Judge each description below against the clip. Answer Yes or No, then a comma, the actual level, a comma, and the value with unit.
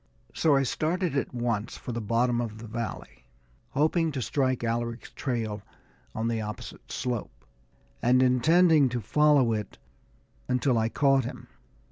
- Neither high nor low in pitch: No, low, 125 Hz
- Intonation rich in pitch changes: No, average, 3.3 semitones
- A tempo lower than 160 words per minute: Yes, average, 145 wpm